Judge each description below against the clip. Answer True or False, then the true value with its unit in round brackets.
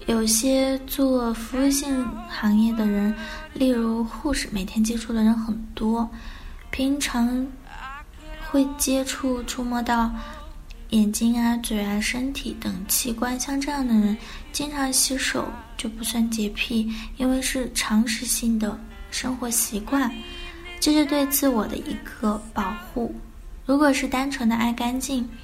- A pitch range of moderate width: True (3.1 semitones)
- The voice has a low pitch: False (240 Hz)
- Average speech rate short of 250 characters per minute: True (200 characters per minute)